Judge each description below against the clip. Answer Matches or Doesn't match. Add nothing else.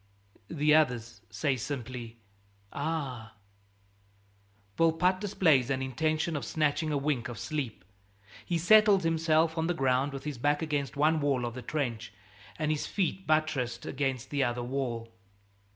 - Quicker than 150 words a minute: Doesn't match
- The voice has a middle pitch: Matches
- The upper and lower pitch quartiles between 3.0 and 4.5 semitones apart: Matches